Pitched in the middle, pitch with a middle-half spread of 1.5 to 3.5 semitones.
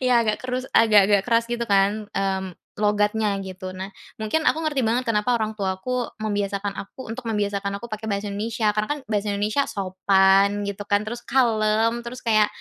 No: high, 215 Hz; narrow, 2.5 semitones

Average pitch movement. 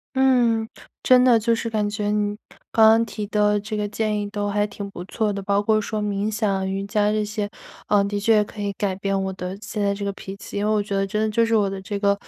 No: narrow, 1.3 semitones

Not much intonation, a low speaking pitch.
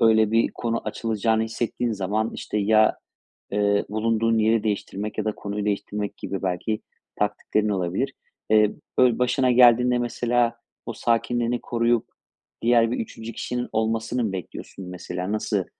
Yes: narrow, 2.2 semitones; low, 110 Hz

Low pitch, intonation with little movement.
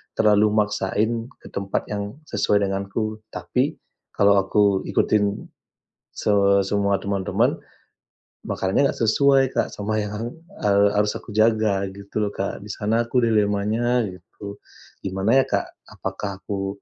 Yes: low, 105 Hz; narrow, 1.6 semitones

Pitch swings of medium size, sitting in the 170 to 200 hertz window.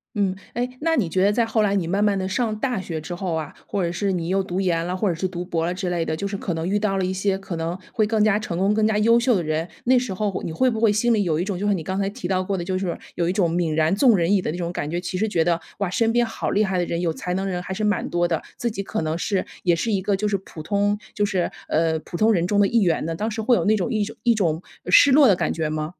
Yes: average, 3.5 semitones; high, 190 Hz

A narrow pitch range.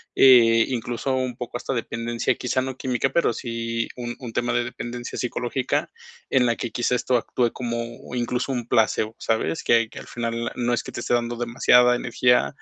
Yes: narrow, 1.1 semitones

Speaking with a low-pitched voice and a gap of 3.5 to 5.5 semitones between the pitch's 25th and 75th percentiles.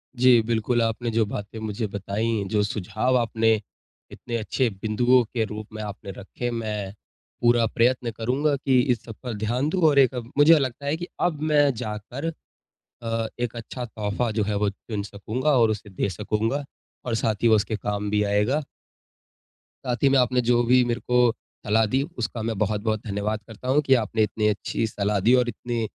No: low, 115 Hz; average, 2.8 semitones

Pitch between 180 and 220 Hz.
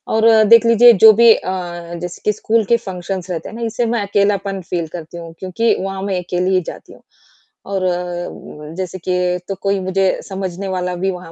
Yes: high, 190 Hz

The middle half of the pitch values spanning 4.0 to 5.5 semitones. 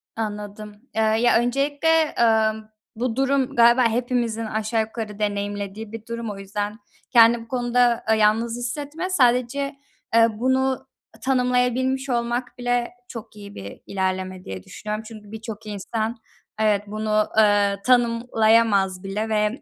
No: narrow, 2.6 semitones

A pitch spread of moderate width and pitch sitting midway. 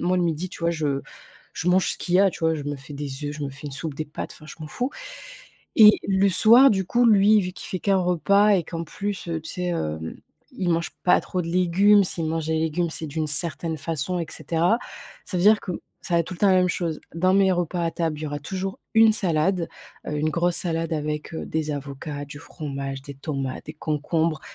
Yes: average, 3.4 semitones; medium, 165 Hz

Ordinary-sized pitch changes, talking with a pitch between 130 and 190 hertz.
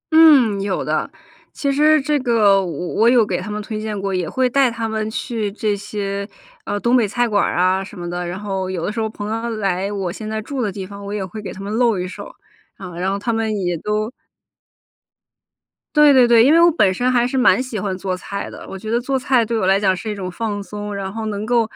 No: average, 3.3 semitones; high, 210 Hz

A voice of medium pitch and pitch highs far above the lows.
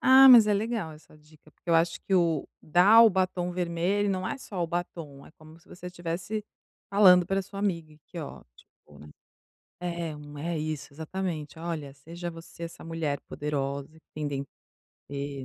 No: medium, 170 Hz; average, 3.5 semitones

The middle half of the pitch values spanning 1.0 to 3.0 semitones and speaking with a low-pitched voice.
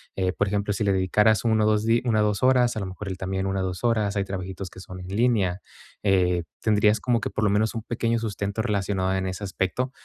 Yes: narrow, 2.6 semitones; low, 100 Hz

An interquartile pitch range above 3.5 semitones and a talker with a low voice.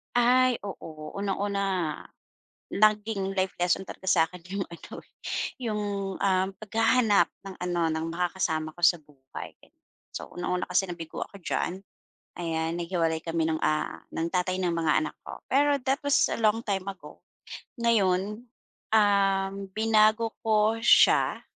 No: average, 4.0 semitones; high, 190 Hz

